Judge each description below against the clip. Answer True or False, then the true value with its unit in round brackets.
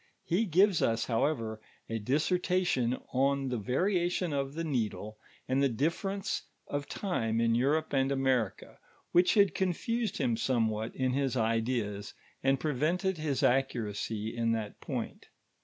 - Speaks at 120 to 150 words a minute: True (140 wpm)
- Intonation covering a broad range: True (6.4 semitones)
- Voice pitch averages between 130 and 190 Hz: True (135 Hz)